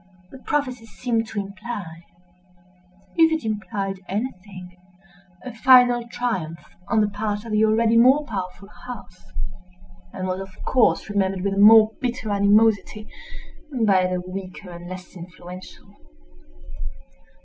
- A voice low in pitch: No, high, 200 Hz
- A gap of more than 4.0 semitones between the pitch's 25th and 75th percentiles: No, average, 3.6 semitones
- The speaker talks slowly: Yes, slow, 120 wpm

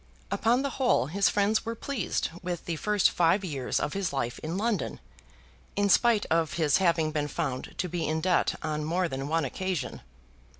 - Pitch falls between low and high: Yes, medium, 170 Hz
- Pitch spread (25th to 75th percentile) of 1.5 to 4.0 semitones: No, average, 4.7 semitones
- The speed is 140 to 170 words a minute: No, average, 185 wpm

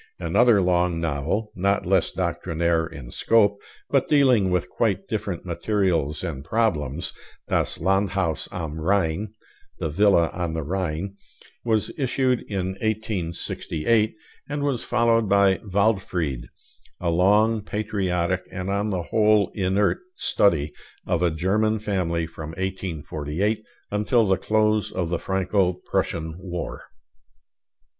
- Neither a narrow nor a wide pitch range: Yes, average, 4.0 semitones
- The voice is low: Yes, very low, 95 Hz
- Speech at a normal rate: No, slow, 120 wpm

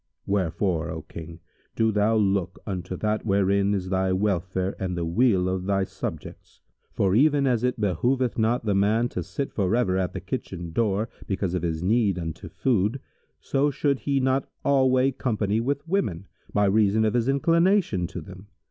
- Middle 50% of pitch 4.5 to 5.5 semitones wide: Yes, average, 4.9 semitones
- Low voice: Yes, low, 100 Hz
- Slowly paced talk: No, average, 175 wpm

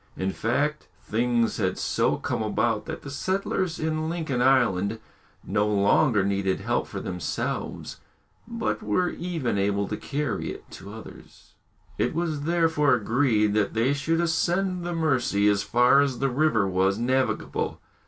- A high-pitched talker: No, low, 125 Hz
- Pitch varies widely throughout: Yes, wide, 7.1 semitones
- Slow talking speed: No, average, 150 wpm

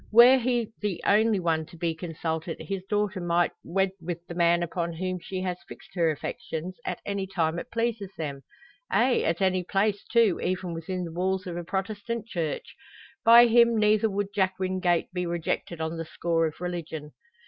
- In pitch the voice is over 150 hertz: Yes, medium, 185 Hz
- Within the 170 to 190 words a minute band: Yes, average, 185 wpm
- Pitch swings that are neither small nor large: Yes, average, 3.3 semitones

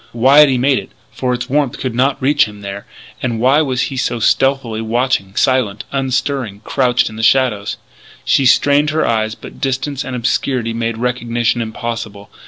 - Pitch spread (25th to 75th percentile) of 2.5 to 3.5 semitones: Yes, average, 2.9 semitones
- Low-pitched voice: Yes, low, 125 Hz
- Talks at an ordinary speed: Yes, average, 185 wpm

